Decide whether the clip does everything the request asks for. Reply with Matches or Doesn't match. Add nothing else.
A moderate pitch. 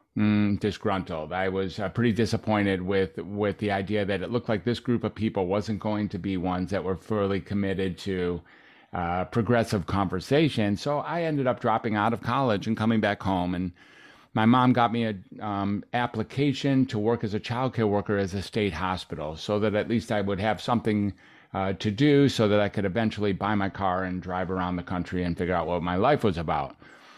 Doesn't match